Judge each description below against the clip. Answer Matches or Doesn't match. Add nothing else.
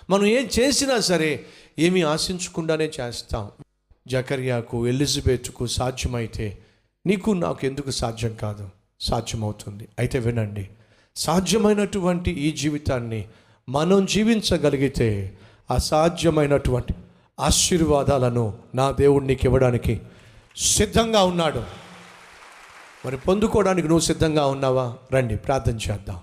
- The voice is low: Matches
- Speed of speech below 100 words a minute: Matches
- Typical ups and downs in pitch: Doesn't match